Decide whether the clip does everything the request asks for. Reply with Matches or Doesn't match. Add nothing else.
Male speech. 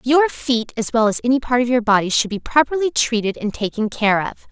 Doesn't match